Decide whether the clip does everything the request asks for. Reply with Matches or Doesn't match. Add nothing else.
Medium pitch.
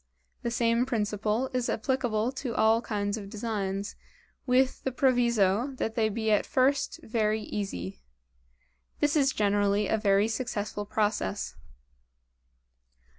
Doesn't match